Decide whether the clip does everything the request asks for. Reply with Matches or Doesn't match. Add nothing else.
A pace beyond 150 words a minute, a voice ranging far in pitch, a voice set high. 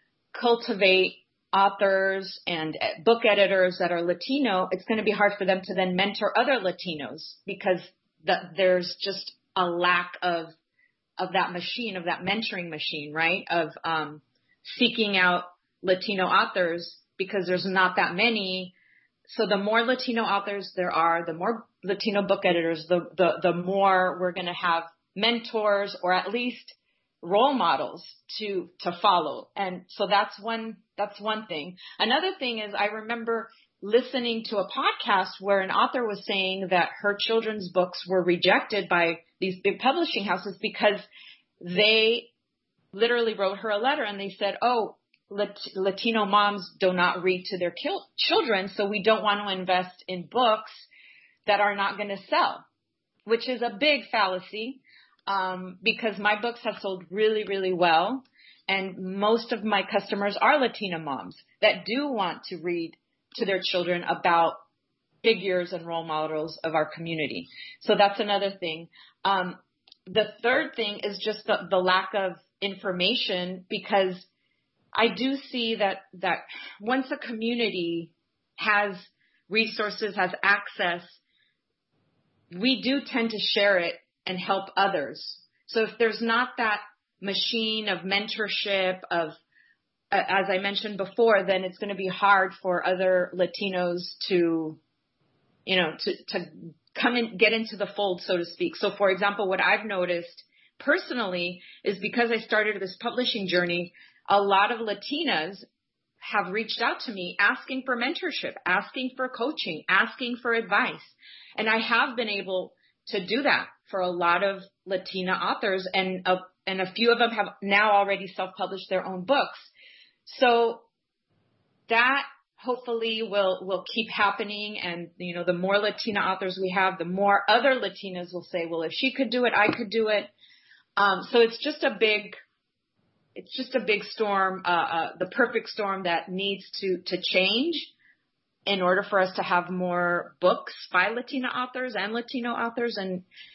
Doesn't match